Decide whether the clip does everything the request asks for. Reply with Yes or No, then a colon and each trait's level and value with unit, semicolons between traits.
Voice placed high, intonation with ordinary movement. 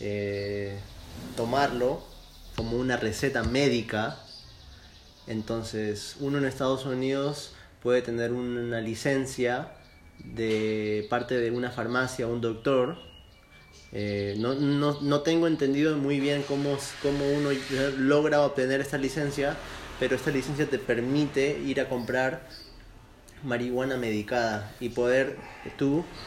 No: low, 125 Hz; average, 3.7 semitones